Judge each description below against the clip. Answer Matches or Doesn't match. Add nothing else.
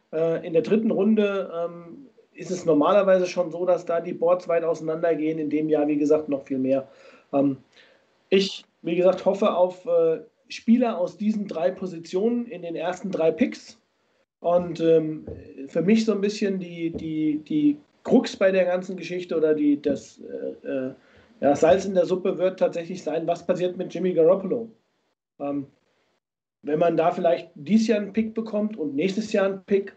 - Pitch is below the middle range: Doesn't match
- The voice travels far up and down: Doesn't match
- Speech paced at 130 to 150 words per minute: Doesn't match